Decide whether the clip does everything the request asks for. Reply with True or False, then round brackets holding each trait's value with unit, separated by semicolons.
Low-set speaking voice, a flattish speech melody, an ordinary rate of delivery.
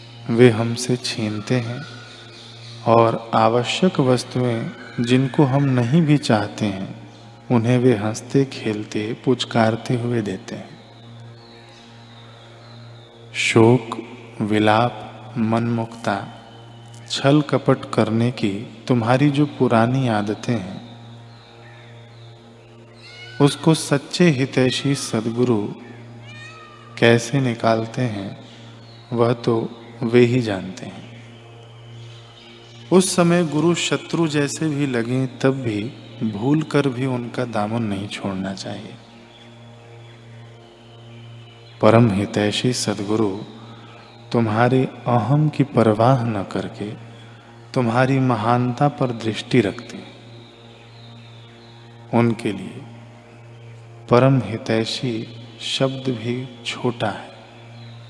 False (115 Hz; 1.4 semitones; 90 wpm)